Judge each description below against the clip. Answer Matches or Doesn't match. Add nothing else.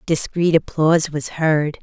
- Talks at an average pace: Doesn't match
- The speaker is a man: Doesn't match